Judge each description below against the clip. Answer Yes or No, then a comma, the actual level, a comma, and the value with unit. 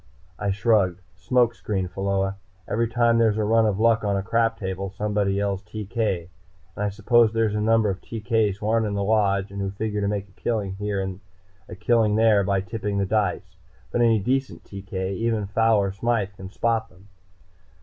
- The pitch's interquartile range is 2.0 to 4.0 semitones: Yes, narrow, 2.5 semitones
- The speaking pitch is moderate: No, low, 105 Hz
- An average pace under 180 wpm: No, average, 200 wpm